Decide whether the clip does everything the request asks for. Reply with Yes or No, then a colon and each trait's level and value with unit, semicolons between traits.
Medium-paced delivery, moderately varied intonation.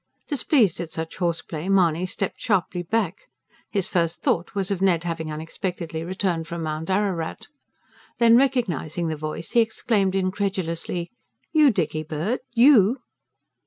No: slow, 130 wpm; average, 3.8 semitones